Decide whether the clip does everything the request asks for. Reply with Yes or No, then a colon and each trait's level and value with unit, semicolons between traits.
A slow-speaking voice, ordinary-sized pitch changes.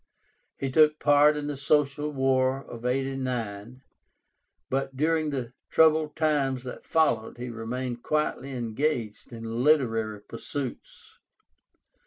Yes: slow, 110 wpm; average, 3.7 semitones